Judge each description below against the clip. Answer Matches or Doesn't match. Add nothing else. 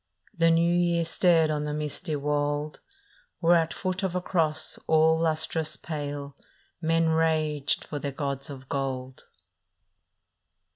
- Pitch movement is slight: Matches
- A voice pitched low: Doesn't match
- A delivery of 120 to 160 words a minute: Matches